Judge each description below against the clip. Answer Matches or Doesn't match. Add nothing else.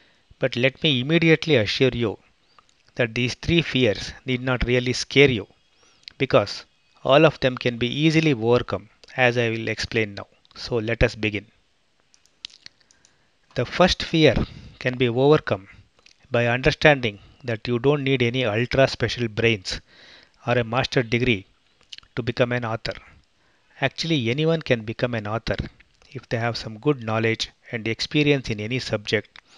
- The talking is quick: Doesn't match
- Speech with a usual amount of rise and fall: Matches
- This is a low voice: Matches